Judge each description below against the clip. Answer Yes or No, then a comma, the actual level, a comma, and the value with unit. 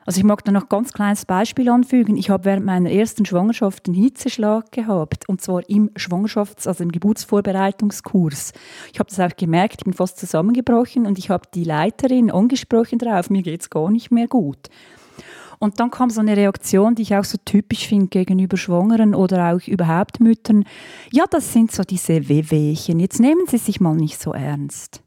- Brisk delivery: Yes, fast, 195 wpm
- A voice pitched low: No, high, 200 Hz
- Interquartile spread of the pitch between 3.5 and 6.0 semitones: Yes, average, 3.8 semitones